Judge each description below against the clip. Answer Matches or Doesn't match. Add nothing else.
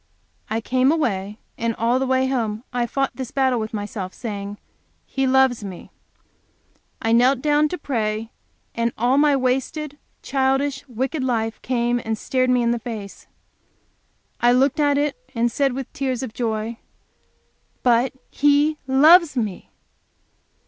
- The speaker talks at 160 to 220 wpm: Doesn't match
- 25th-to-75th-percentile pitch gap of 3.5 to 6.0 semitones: Doesn't match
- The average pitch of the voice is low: Doesn't match